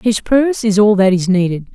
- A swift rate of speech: Yes, fast, 240 wpm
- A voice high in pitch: Yes, high, 205 Hz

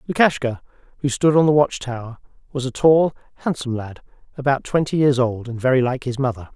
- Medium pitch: No, low, 130 Hz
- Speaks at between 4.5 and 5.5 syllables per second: No, 6.0 syllables/s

